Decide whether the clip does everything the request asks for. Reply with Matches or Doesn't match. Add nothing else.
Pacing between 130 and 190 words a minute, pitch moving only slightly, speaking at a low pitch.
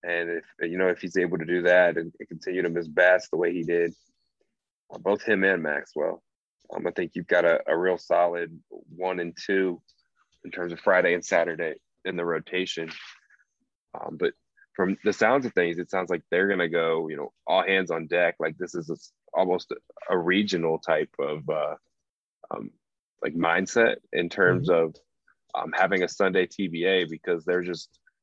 Matches